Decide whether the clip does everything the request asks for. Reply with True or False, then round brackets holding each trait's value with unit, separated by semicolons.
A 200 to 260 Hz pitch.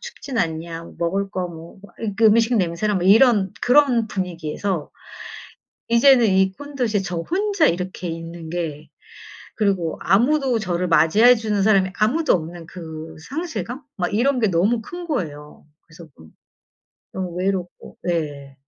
False (190 Hz)